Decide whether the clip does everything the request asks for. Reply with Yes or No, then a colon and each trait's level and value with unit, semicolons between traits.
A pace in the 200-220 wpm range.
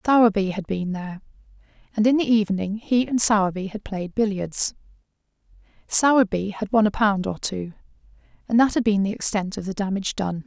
No: average, 180 wpm